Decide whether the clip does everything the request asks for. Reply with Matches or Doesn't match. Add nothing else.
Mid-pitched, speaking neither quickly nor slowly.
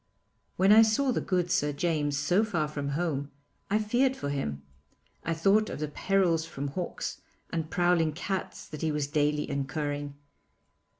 Matches